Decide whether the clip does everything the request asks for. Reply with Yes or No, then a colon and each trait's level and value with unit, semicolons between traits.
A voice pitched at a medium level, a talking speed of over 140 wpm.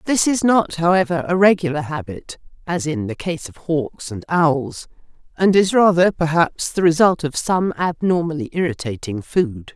Yes: medium, 160 Hz; average, 160 wpm